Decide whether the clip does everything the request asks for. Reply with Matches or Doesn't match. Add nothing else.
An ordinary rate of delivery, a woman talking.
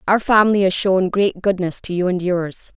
Doesn't match